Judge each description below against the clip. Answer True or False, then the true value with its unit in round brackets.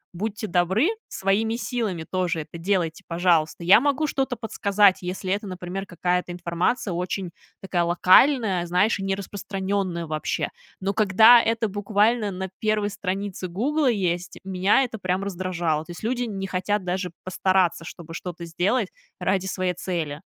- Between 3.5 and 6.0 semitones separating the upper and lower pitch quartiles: False (2.9 semitones)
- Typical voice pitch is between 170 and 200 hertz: True (190 Hz)